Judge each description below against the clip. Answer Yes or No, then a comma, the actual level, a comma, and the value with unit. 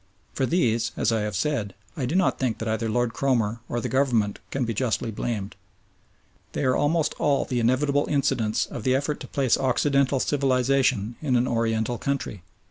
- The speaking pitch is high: No, low, 125 Hz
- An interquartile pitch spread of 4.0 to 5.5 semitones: No, average, 3.4 semitones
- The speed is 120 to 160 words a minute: No, average, 185 wpm